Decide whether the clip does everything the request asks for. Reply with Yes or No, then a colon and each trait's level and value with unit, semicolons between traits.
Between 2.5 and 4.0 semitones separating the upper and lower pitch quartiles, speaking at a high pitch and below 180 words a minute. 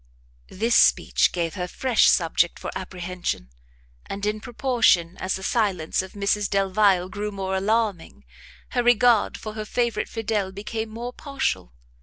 Yes: average, 3.4 semitones; high, 205 Hz; average, 145 wpm